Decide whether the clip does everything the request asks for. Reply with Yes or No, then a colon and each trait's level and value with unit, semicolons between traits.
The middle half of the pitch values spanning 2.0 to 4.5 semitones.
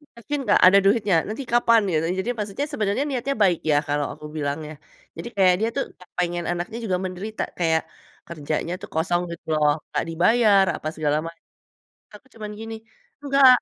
No: average, 5.2 semitones